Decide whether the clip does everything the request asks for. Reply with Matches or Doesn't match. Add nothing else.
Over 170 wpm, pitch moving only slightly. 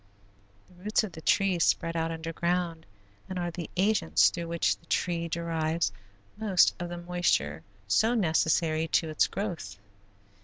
Doesn't match